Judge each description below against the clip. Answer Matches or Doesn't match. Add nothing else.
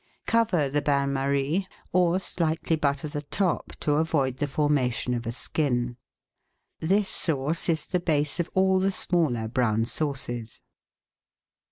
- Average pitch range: Matches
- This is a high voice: Doesn't match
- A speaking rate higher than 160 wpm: Doesn't match